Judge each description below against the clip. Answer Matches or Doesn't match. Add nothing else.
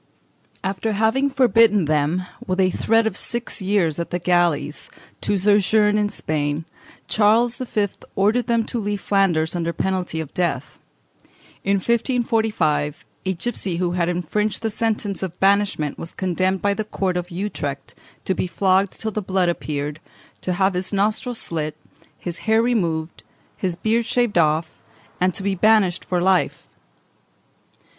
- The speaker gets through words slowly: Doesn't match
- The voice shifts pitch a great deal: Doesn't match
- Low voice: Doesn't match